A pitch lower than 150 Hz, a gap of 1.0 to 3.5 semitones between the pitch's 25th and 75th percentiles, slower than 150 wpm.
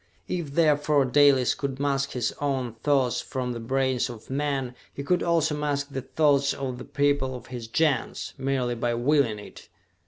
No: low, 135 Hz; narrow, 2.5 semitones; average, 175 wpm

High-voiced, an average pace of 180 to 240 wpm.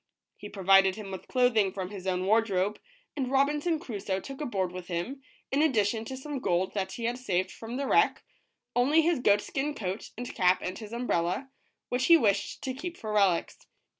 Yes: high, 220 Hz; average, 195 wpm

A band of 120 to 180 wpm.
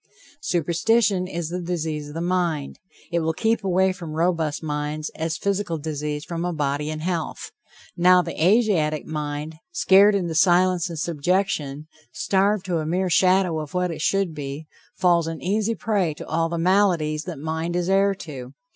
Yes: average, 175 wpm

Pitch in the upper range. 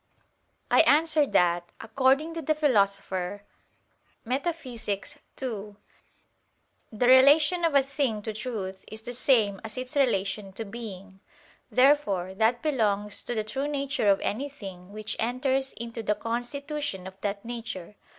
Yes: high, 230 Hz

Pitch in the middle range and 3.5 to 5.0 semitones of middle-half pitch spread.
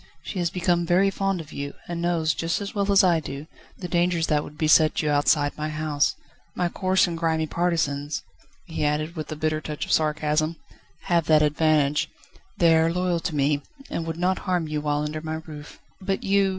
No: medium, 160 Hz; narrow, 2.5 semitones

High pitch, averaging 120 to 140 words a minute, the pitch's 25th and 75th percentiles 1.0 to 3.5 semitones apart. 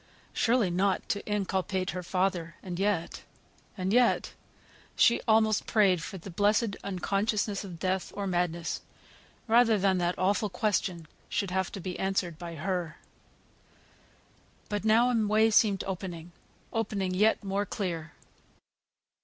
Yes: high, 195 Hz; slow, 135 wpm; average, 2.8 semitones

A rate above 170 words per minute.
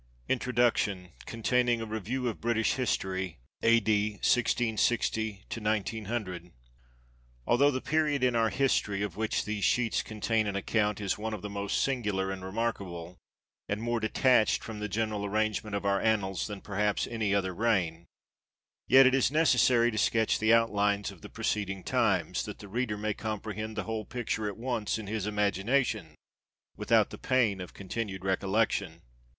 No: average, 155 wpm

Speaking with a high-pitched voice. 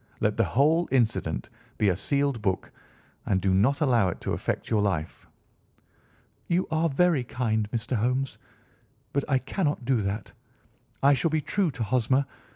No: low, 125 Hz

